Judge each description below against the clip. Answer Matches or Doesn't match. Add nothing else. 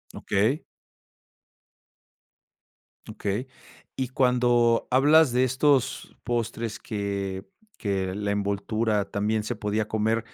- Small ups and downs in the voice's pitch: Doesn't match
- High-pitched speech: Doesn't match